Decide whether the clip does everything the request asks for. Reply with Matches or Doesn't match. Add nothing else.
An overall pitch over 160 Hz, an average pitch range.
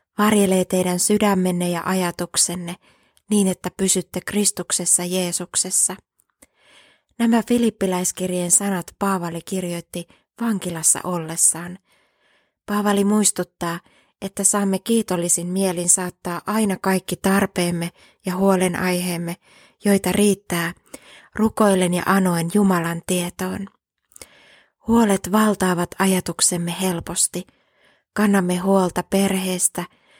Doesn't match